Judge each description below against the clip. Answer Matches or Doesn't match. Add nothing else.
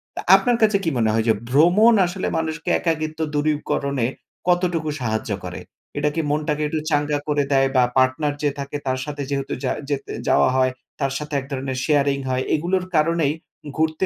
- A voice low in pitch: Doesn't match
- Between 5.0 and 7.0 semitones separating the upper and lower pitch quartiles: Doesn't match